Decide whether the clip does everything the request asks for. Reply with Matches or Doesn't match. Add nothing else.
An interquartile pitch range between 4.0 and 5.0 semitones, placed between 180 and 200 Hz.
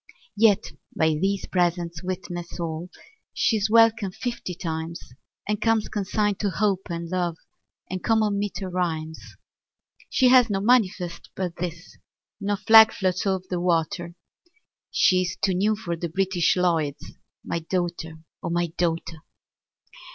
Doesn't match